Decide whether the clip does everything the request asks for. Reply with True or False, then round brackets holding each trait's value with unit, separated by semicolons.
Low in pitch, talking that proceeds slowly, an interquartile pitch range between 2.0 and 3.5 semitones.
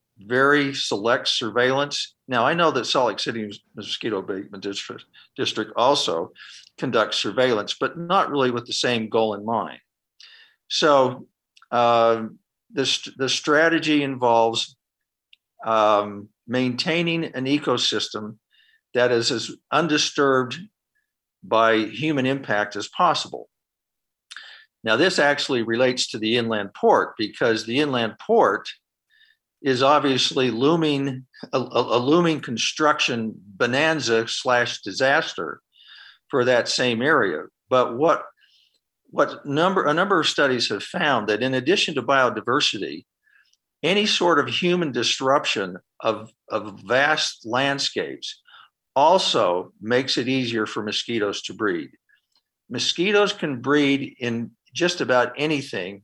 False (130 Hz; 115 wpm; 5.4 semitones)